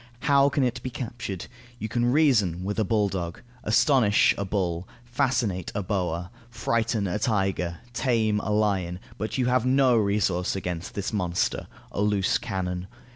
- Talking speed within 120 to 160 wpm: Yes, average, 155 wpm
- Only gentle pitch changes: No, average, 4.5 semitones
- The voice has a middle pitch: No, low, 105 Hz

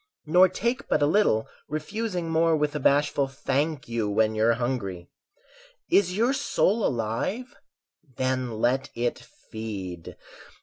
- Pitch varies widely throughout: Yes, wide, 7.9 semitones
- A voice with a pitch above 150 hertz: No, low, 135 Hz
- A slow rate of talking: Yes, slow, 130 wpm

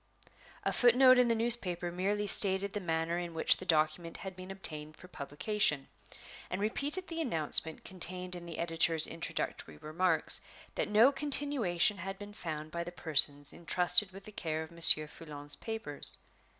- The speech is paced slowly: No, average, 165 wpm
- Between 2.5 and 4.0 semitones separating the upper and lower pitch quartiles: No, average, 4.4 semitones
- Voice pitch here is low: No, medium, 180 Hz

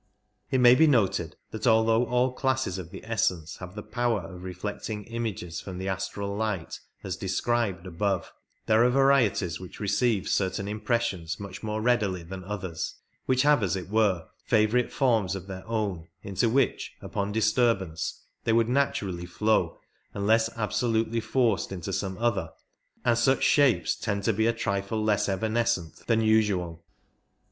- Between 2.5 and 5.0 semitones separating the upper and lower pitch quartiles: Yes, average, 3.7 semitones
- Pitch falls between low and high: No, low, 105 Hz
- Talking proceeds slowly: No, average, 160 wpm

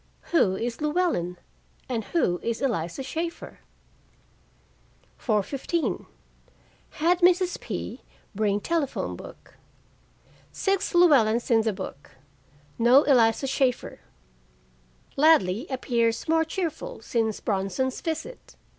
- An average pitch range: No, wide, 6.8 semitones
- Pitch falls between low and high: No, very high, 260 Hz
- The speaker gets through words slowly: Yes, slow, 95 wpm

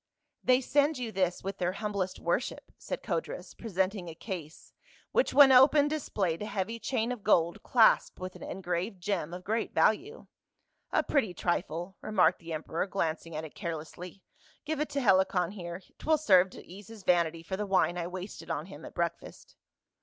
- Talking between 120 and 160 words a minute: No, average, 185 wpm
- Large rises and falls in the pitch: No, average, 4.6 semitones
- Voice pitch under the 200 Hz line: Yes, high, 190 Hz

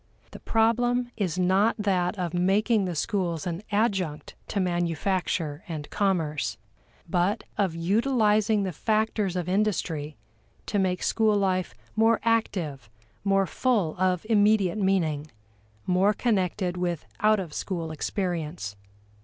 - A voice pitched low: No, high, 190 Hz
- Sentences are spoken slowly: Yes, slow, 125 wpm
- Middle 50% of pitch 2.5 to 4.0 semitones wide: Yes, average, 3.6 semitones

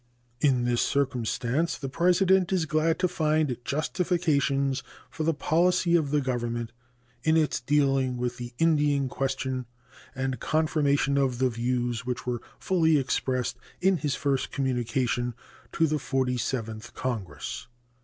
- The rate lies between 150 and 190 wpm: No, slow, 135 wpm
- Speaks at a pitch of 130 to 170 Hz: Yes, low, 135 Hz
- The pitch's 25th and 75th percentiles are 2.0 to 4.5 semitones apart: Yes, average, 4.0 semitones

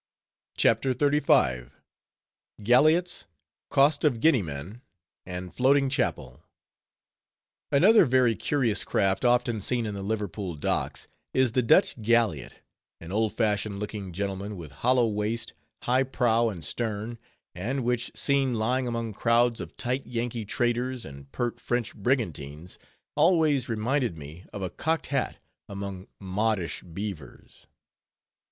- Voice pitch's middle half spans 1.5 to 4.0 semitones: No, average, 4.6 semitones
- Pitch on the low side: Yes, low, 115 Hz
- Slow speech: Yes, slow, 125 wpm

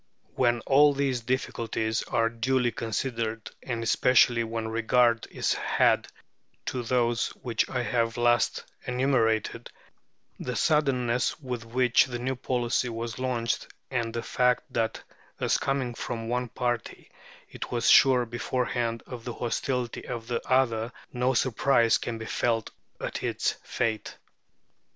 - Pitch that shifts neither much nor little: No, narrow, 1.6 semitones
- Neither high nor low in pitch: No, low, 120 Hz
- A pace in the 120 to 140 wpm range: Yes, slow, 135 wpm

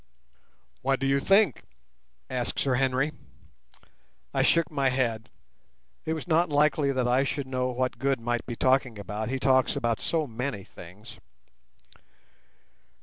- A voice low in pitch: Yes, low, 130 Hz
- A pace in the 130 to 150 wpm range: Yes, average, 145 wpm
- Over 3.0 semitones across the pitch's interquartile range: No, narrow, 2.6 semitones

